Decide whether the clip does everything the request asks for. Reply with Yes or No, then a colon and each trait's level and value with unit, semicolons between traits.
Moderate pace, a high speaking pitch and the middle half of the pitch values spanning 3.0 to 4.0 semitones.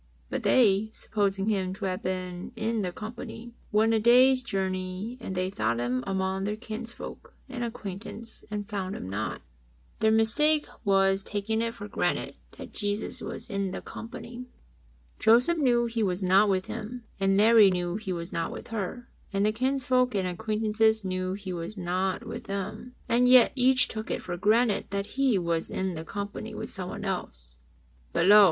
Yes: average, 180 wpm; high, 205 Hz; average, 3.5 semitones